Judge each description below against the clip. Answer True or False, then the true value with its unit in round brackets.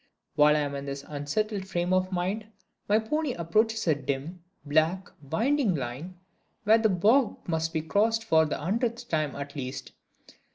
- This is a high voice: False (175 Hz)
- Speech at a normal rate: True (165 wpm)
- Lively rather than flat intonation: True (6.6 semitones)